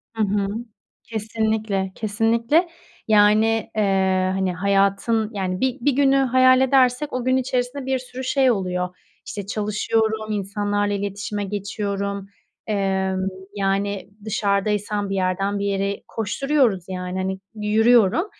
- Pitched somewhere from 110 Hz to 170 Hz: No, high, 205 Hz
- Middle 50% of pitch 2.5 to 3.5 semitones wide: Yes, average, 2.9 semitones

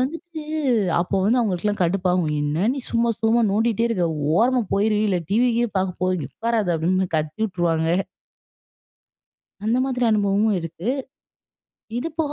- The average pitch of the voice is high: Yes, high, 210 Hz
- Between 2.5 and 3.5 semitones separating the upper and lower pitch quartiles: No, average, 4.6 semitones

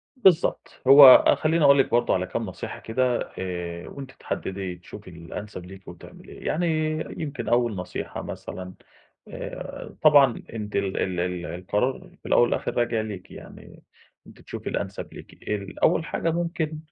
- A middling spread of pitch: No, wide, 7.2 semitones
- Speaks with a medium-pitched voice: No, low, 110 Hz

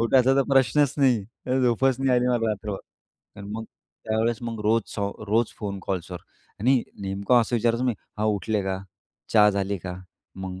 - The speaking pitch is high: No, low, 110 Hz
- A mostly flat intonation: No, average, 3.4 semitones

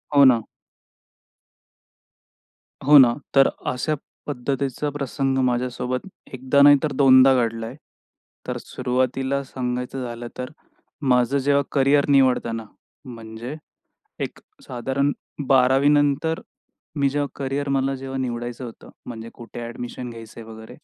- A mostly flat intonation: Yes, narrow, 2.3 semitones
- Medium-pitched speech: No, low, 130 Hz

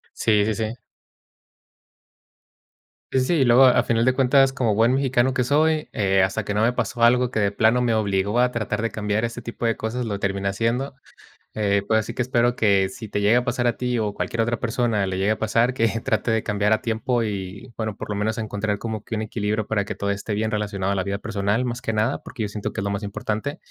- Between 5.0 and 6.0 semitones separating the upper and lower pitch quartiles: No, average, 2.9 semitones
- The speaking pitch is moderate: No, low, 110 Hz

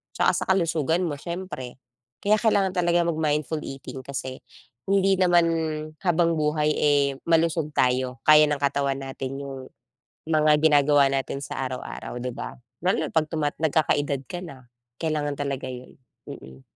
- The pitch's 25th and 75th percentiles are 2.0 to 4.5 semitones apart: Yes, average, 3.4 semitones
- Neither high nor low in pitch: Yes, medium, 150 Hz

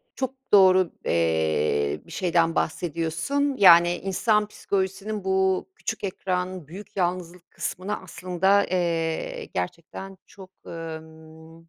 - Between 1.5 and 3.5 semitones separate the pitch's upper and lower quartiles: Yes, average, 2.9 semitones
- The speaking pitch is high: No, medium, 180 Hz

